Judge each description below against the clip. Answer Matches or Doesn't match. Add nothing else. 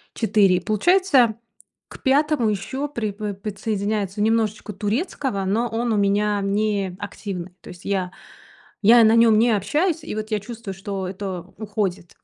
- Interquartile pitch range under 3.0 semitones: Matches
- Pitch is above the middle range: Matches